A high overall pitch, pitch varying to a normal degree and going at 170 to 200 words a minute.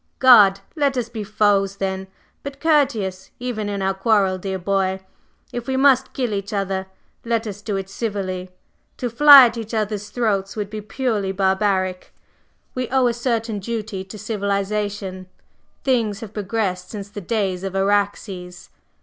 No: high, 205 Hz; average, 3.2 semitones; average, 160 wpm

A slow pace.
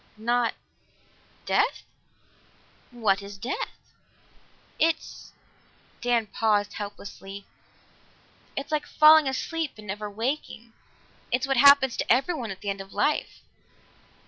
Yes: slow, 115 wpm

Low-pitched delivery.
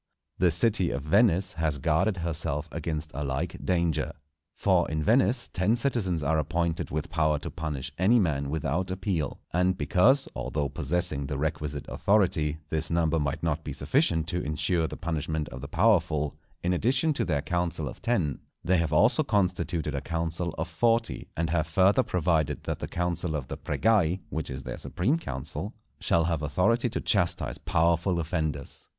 Yes: very low, 85 Hz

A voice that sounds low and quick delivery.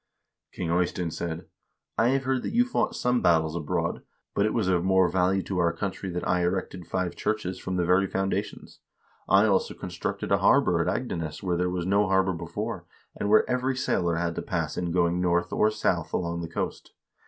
Yes: very low, 90 Hz; fast, 210 wpm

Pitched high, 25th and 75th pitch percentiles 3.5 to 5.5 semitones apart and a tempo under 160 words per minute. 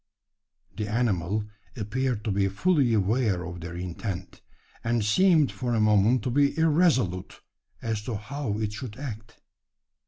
No: low, 110 Hz; average, 4.2 semitones; average, 145 wpm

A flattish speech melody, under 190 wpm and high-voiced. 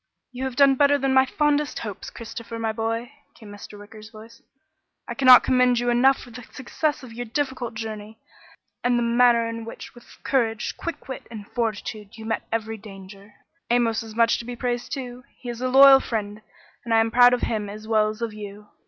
No: narrow, 2.3 semitones; fast, 205 wpm; high, 230 Hz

